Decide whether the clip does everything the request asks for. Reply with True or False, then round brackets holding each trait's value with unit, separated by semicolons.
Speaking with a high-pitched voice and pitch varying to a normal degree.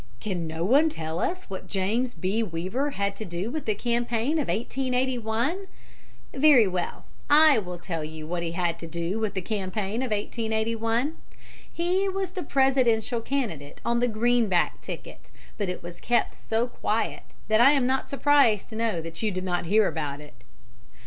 False (220 Hz; 6.0 semitones)